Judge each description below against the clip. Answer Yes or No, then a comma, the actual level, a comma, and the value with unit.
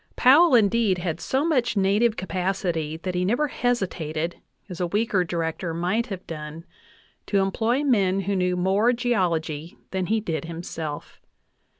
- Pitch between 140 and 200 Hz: Yes, high, 190 Hz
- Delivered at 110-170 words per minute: Yes, average, 150 wpm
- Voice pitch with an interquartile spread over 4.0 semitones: Yes, average, 5.0 semitones